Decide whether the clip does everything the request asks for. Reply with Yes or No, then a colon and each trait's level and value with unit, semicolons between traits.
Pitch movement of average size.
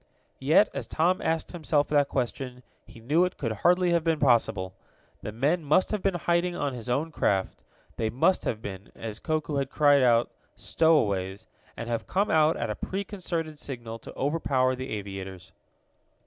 No: wide, 6.3 semitones